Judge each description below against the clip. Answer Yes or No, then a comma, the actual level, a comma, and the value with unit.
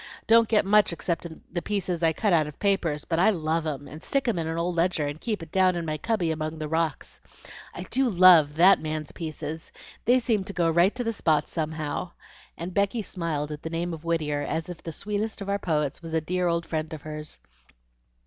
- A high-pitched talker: No, medium, 170 Hz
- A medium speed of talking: No, fast, 225 wpm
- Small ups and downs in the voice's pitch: No, average, 3.6 semitones